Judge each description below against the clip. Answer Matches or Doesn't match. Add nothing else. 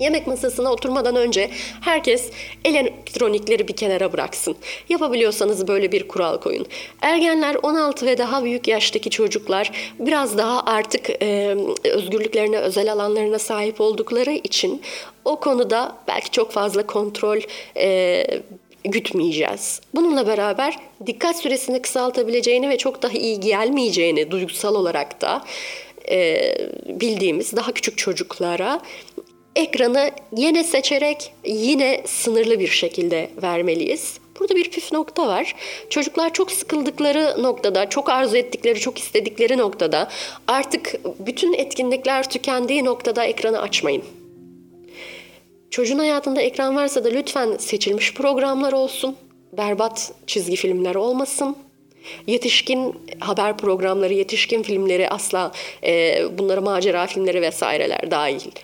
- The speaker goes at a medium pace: Matches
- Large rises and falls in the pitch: Matches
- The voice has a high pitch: Matches